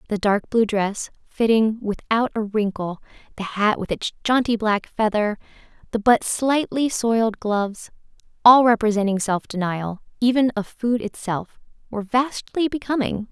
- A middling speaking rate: No, slow, 130 wpm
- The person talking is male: No, female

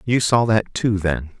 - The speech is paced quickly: Yes, fast, 215 wpm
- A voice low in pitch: Yes, low, 105 Hz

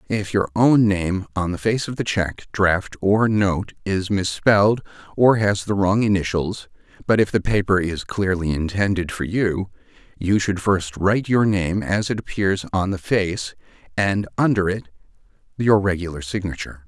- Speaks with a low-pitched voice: Yes, very low, 95 Hz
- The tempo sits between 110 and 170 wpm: Yes, average, 165 wpm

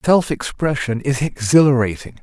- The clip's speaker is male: Yes, male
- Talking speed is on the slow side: Yes, slow, 110 wpm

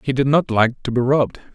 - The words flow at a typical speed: No, fast, 275 wpm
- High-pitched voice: No, low, 130 Hz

